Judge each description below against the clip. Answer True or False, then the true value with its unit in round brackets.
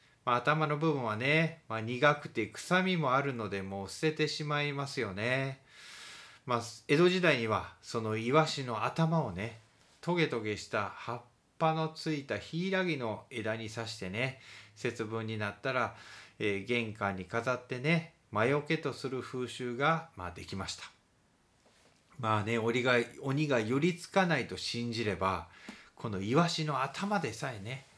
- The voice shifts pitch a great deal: True (5.7 semitones)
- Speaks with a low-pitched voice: True (125 Hz)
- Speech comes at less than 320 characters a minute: True (285 characters per minute)